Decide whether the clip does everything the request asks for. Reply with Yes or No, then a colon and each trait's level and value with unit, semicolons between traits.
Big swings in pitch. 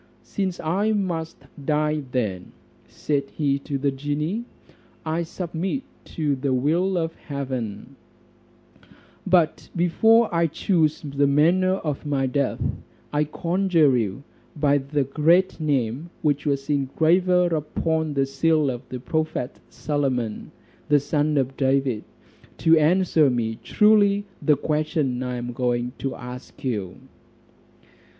No: average, 3.7 semitones